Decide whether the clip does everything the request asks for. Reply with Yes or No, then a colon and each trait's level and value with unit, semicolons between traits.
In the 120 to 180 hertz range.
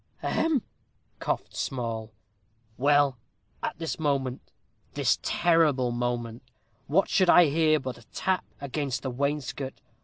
Yes: medium, 140 Hz